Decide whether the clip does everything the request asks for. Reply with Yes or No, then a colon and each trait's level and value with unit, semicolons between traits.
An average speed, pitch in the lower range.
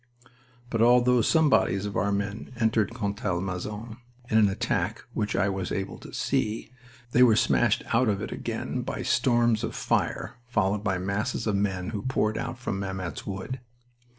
Yes: average, 170 wpm; low, 105 Hz